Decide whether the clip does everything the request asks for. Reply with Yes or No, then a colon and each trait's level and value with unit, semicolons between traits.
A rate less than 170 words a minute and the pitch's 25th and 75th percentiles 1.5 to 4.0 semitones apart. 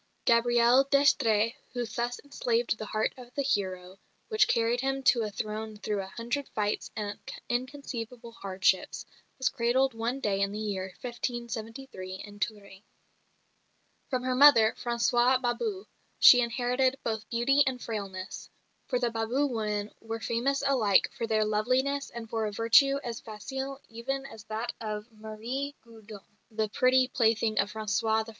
Yes: average, 150 wpm; average, 3.0 semitones